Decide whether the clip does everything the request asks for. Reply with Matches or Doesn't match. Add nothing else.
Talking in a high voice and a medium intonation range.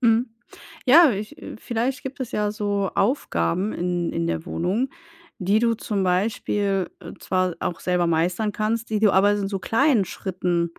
Matches